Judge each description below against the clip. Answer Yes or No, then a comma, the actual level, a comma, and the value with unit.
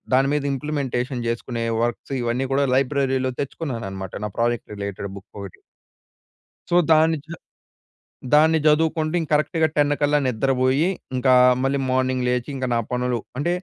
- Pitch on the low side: Yes, low, 130 Hz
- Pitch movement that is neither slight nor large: Yes, average, 3.6 semitones